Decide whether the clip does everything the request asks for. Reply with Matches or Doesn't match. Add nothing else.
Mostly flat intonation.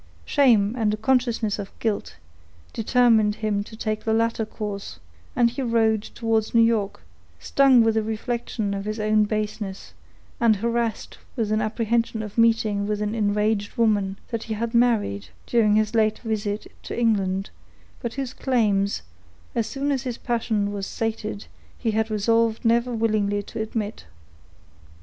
Matches